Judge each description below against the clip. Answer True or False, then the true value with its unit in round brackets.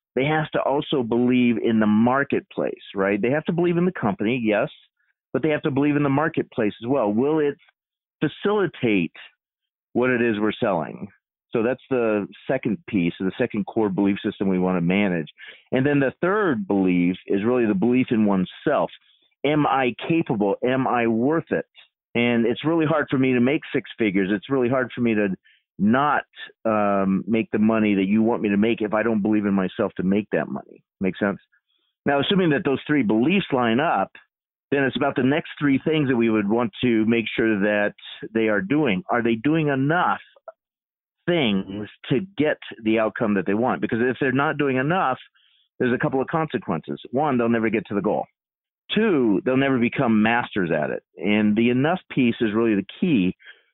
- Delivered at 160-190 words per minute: False (200 wpm)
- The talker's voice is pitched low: True (120 Hz)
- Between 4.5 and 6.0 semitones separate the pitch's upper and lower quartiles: True (4.8 semitones)